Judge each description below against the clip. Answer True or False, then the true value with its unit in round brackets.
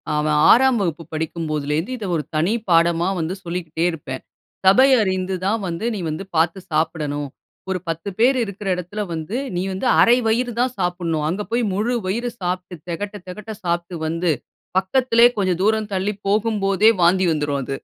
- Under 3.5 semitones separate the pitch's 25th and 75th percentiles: False (4.3 semitones)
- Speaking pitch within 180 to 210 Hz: True (185 Hz)